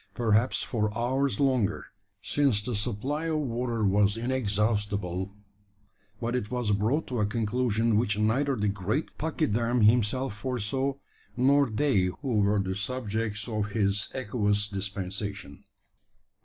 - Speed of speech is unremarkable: No, slow, 130 wpm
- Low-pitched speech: Yes, low, 110 Hz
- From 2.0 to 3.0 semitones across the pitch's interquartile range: No, average, 3.7 semitones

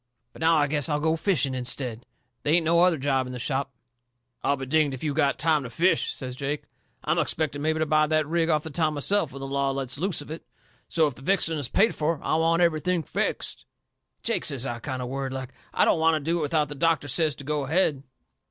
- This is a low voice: No, medium, 150 Hz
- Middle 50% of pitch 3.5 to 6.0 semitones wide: No, average, 3.0 semitones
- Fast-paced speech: Yes, fast, 245 wpm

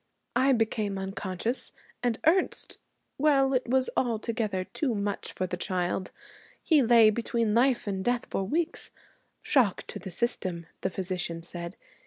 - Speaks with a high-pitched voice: Yes, high, 220 Hz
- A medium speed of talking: Yes, average, 145 wpm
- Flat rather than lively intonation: No, average, 4.7 semitones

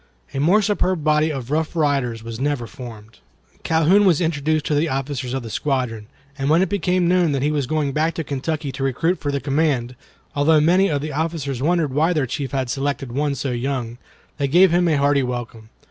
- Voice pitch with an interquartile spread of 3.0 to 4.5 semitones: Yes, average, 3.5 semitones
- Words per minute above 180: Yes, fast, 205 wpm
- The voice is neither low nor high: Yes, medium, 145 Hz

